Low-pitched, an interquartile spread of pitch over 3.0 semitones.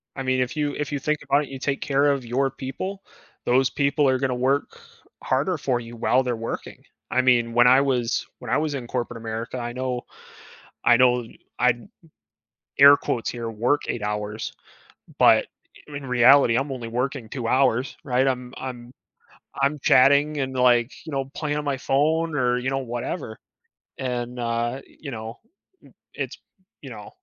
No: low, 130 Hz; narrow, 2.4 semitones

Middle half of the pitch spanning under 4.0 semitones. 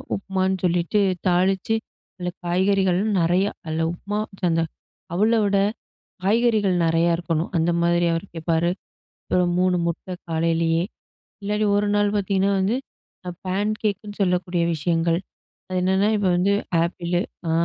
Yes: average, 2.7 semitones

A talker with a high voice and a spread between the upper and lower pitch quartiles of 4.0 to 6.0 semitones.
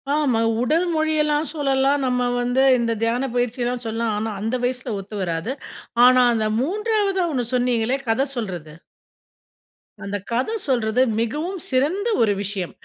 Yes: very high, 250 Hz; average, 4.4 semitones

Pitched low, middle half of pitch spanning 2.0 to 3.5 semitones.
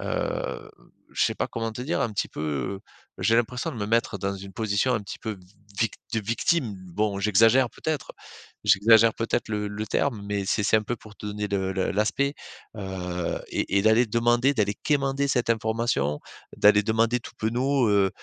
Yes: low, 110 Hz; average, 2.8 semitones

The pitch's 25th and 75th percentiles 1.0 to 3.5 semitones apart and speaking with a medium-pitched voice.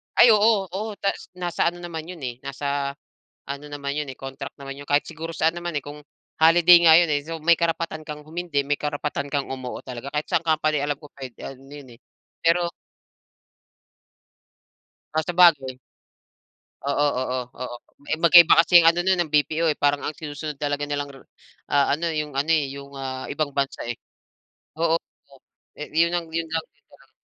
Yes: average, 2.9 semitones; medium, 150 Hz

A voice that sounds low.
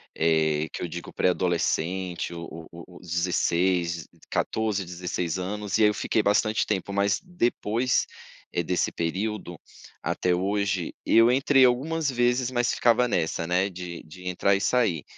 Yes: very low, 95 Hz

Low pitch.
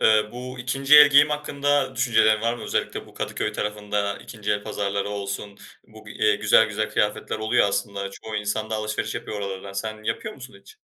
Yes: low, 110 Hz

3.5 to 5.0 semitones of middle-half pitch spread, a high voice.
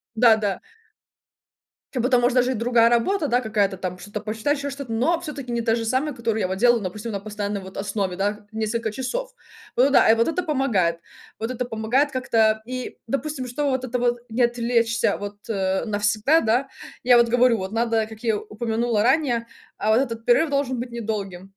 No: average, 3.0 semitones; high, 230 Hz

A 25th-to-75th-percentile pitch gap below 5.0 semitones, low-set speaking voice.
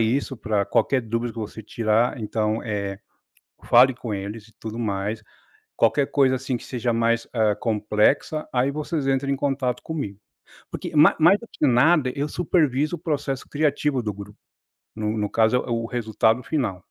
Yes: average, 4.2 semitones; low, 120 Hz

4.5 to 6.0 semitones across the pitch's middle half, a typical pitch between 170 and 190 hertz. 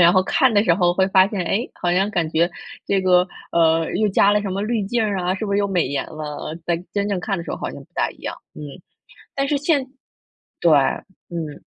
No: average, 3.3 semitones; medium, 185 Hz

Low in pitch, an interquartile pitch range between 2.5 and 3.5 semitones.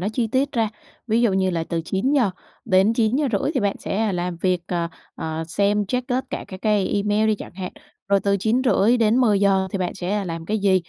No: high, 200 Hz; average, 3.2 semitones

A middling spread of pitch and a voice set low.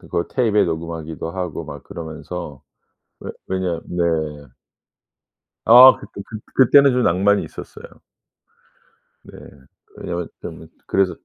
Yes: average, 4.2 semitones; very low, 90 Hz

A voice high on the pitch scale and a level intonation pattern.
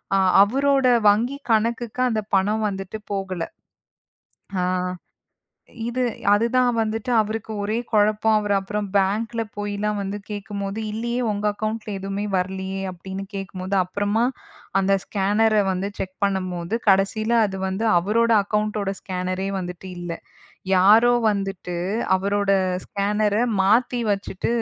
Yes: high, 205 Hz; narrow, 2.2 semitones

